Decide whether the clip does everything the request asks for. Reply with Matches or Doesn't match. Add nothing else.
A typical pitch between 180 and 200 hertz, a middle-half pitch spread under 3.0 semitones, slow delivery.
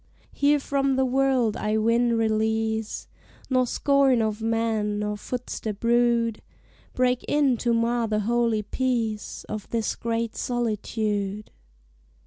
Doesn't match